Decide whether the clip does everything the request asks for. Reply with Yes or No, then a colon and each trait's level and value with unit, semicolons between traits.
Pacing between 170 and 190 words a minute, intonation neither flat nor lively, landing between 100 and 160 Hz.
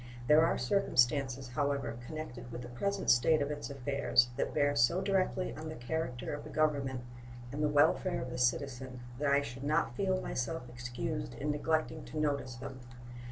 Yes: average, 180 wpm; average, 3.8 semitones; medium, 140 Hz